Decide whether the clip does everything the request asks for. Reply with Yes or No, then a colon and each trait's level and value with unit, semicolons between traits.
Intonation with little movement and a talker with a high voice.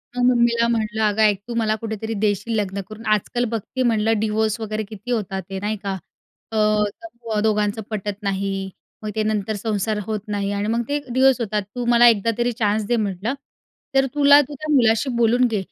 Yes: narrow, 2.3 semitones; high, 220 Hz